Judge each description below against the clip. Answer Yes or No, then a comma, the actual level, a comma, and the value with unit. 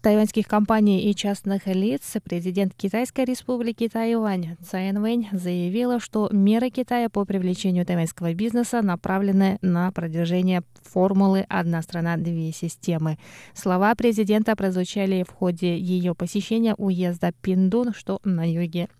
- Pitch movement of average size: Yes, average, 3.4 semitones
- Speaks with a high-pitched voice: Yes, high, 195 Hz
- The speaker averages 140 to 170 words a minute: No, average, 125 wpm